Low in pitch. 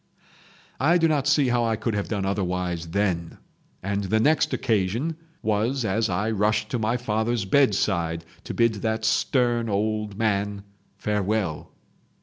Yes: low, 110 Hz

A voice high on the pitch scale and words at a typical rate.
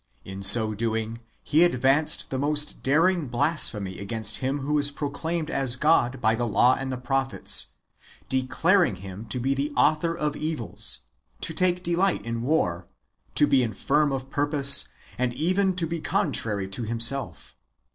No: low, 135 Hz; average, 160 wpm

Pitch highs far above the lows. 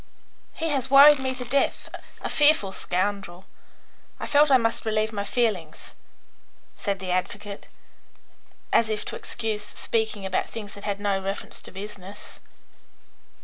No: average, 3.6 semitones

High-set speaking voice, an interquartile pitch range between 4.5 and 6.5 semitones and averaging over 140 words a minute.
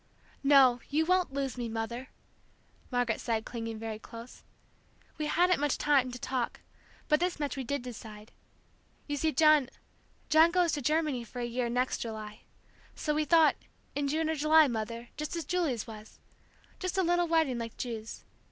Yes: very high, 270 Hz; average, 4.9 semitones; average, 170 wpm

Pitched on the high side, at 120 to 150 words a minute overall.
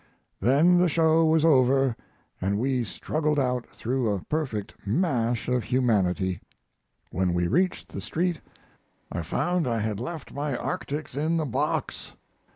No: low, 130 Hz; average, 145 wpm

